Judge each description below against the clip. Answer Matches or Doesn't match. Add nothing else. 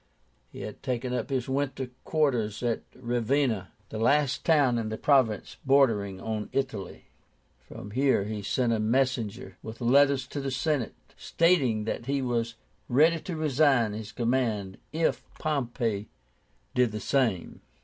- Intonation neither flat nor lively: Matches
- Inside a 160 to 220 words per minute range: Doesn't match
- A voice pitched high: Doesn't match